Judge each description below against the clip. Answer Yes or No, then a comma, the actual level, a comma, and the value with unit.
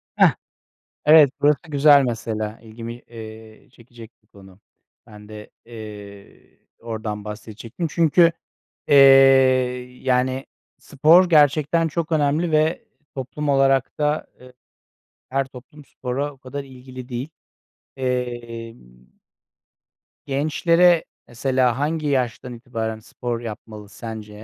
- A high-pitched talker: No, low, 125 Hz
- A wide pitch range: No, average, 4.4 semitones